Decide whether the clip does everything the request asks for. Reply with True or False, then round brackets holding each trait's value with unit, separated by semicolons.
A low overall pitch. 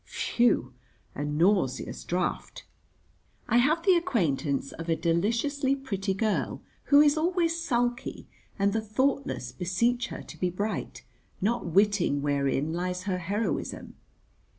False (200 Hz)